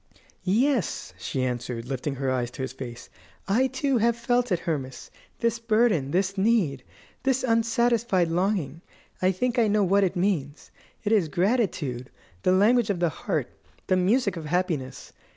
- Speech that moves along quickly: No, average, 160 wpm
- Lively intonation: Yes, wide, 8.3 semitones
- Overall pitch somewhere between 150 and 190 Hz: Yes, medium, 185 Hz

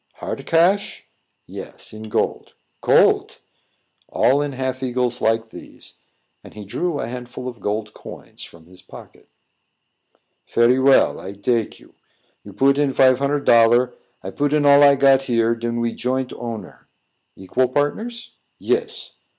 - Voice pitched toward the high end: No, low, 125 Hz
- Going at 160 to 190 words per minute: No, average, 150 wpm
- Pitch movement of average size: Yes, average, 3.5 semitones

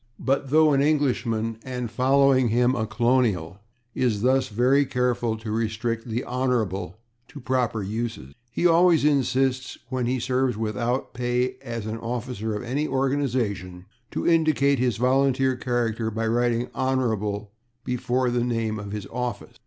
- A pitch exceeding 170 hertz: No, low, 125 Hz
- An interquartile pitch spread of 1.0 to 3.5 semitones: Yes, average, 2.8 semitones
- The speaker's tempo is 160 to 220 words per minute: No, average, 145 wpm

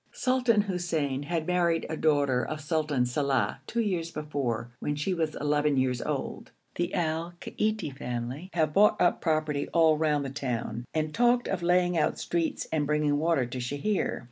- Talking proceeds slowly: No, average, 170 wpm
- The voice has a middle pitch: Yes, medium, 155 Hz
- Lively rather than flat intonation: No, average, 3.6 semitones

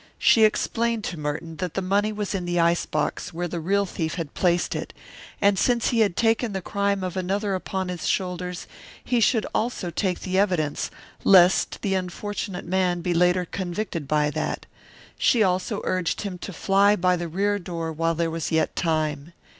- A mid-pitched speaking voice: Yes, medium, 180 Hz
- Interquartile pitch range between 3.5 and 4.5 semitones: No, average, 2.9 semitones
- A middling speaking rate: Yes, average, 190 wpm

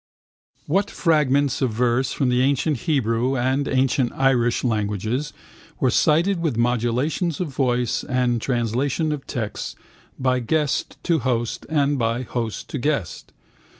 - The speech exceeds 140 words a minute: No, slow, 135 wpm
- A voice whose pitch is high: No, low, 130 Hz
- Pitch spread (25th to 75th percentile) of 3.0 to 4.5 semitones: Yes, average, 3.3 semitones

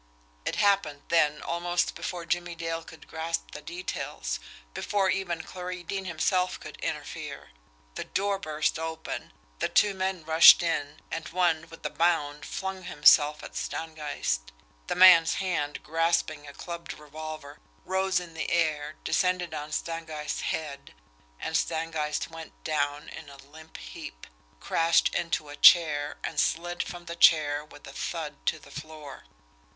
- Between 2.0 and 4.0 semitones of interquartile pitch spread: Yes, narrow, 2.6 semitones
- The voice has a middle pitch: Yes, medium, 160 Hz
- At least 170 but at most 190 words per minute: No, average, 145 wpm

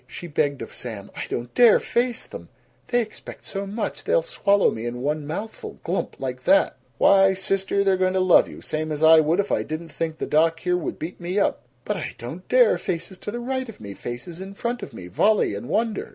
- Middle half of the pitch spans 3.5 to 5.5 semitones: Yes, average, 5.1 semitones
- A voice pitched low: No, medium, 180 Hz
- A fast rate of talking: Yes, fast, 235 wpm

